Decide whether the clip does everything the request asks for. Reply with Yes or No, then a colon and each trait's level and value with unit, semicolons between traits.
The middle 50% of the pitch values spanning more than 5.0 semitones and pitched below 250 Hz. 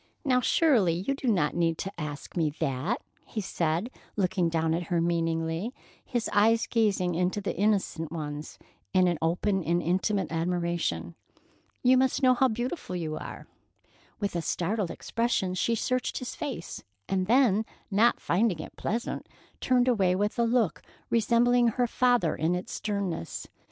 Yes: wide, 5.6 semitones; high, 190 Hz